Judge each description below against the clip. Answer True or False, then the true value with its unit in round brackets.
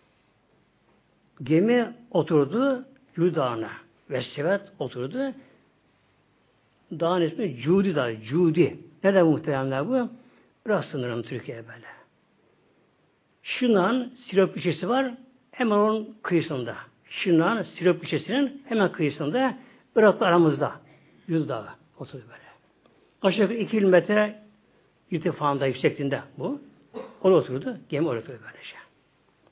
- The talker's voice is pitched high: False (180 Hz)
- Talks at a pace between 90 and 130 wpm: True (95 wpm)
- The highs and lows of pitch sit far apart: True (6.7 semitones)